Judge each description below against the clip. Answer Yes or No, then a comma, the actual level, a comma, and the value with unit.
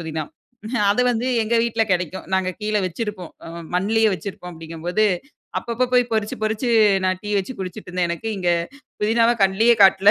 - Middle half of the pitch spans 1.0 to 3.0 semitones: No, average, 3.6 semitones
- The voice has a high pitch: Yes, high, 200 Hz